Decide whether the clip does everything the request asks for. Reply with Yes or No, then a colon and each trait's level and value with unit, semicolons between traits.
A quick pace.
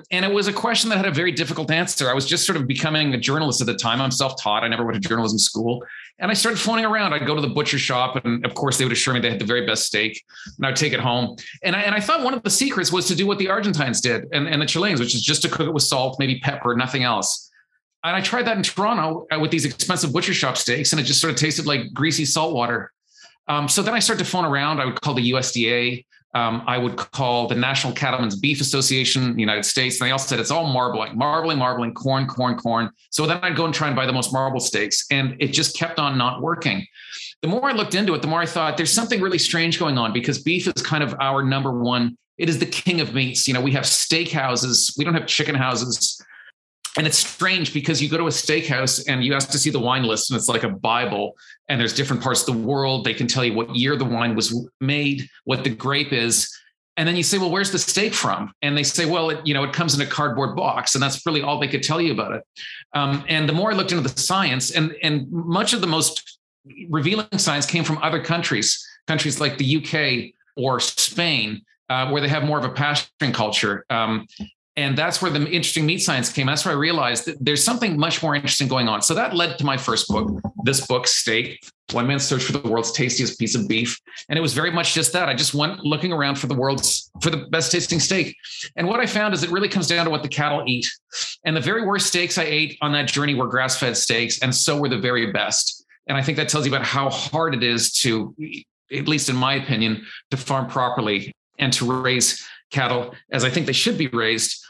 Yes: fast, 255 wpm